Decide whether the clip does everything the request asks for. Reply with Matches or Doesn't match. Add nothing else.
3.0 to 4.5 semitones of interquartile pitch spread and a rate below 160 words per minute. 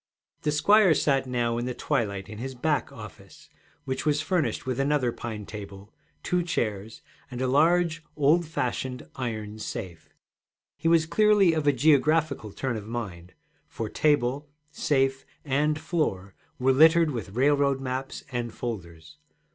Doesn't match